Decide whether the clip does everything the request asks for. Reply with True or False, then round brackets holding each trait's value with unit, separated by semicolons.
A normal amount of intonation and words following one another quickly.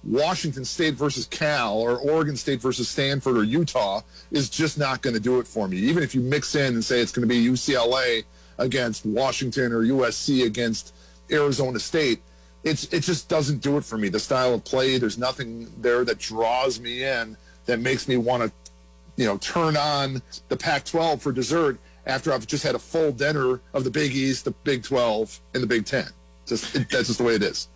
True (3.9 semitones; 210 wpm)